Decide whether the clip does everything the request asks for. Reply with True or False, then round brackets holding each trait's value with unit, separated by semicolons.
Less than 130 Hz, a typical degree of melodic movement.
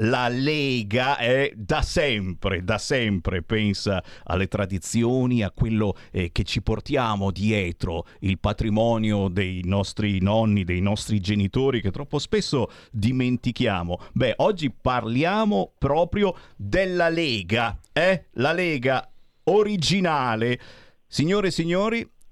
True (110 Hz; 4.8 semitones)